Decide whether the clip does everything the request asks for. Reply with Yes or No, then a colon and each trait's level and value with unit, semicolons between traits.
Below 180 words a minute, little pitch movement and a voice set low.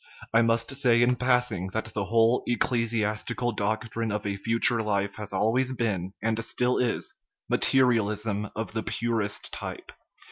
Yes: average, 150 wpm; narrow, 2.2 semitones; low, 115 Hz